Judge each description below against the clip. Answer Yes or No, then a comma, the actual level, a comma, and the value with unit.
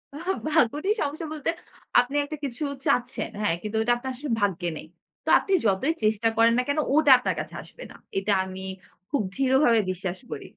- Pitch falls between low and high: No, high, 245 Hz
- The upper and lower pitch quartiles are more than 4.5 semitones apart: Yes, average, 5.3 semitones